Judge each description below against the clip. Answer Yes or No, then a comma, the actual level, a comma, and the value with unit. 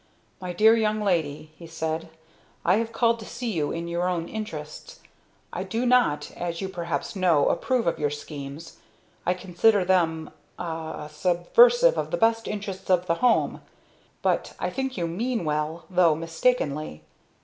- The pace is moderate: Yes, average, 160 wpm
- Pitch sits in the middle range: Yes, medium, 175 Hz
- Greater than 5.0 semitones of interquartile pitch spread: Yes, wide, 5.5 semitones